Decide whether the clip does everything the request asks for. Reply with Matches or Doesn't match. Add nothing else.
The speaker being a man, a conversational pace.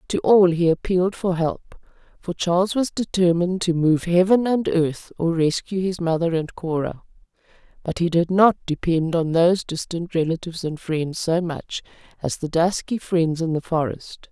Doesn't match